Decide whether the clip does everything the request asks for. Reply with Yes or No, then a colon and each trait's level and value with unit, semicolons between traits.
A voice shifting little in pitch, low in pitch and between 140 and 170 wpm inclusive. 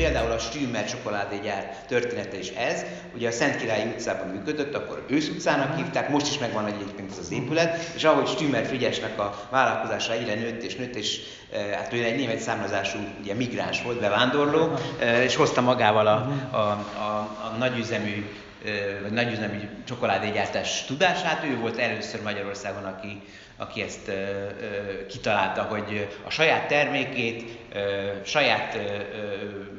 No: average, 3.6 semitones; low, 105 Hz; average, 150 wpm